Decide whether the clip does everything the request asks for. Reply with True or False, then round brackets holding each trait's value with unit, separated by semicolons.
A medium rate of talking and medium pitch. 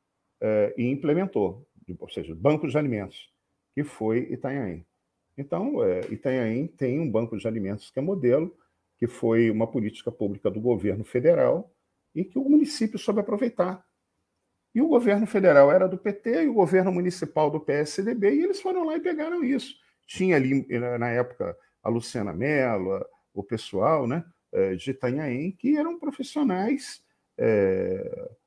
True (150 wpm; 165 Hz)